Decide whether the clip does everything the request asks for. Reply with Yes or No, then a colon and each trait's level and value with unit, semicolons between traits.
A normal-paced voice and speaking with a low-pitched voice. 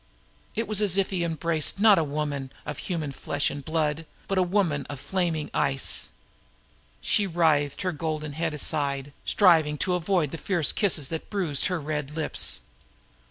No: average, 165 wpm; medium, 160 Hz